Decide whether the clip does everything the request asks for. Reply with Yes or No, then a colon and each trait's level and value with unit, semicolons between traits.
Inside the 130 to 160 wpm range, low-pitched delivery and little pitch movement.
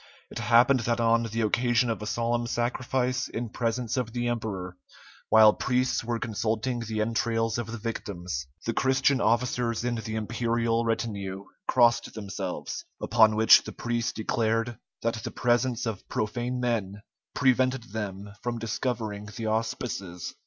Yes: average, 145 wpm; low, 115 Hz; narrow, 1.8 semitones